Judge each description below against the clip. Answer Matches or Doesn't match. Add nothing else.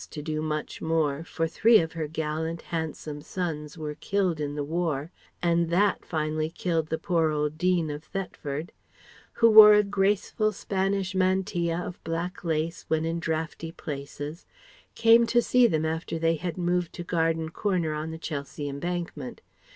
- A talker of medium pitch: Matches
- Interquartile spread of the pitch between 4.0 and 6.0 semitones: Doesn't match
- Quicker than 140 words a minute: Matches